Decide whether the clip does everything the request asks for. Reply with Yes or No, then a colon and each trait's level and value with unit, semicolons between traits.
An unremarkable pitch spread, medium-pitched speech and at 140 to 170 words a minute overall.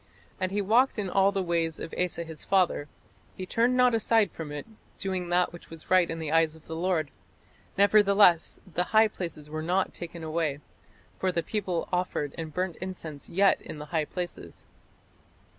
No: average, 3.1 semitones; medium, 175 Hz; average, 185 wpm